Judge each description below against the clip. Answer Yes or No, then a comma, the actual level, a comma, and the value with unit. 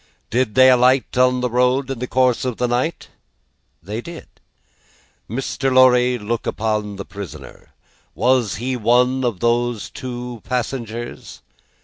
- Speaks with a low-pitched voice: Yes, low, 125 Hz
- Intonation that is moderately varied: No, narrow, 1.7 semitones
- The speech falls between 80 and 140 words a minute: Yes, slow, 135 wpm